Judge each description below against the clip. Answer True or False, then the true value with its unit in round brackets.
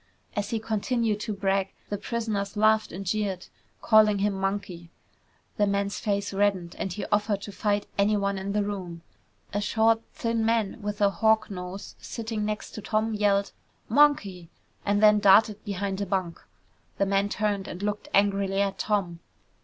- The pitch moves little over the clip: True (1.5 semitones)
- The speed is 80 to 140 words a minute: False (165 wpm)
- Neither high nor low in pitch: False (205 Hz)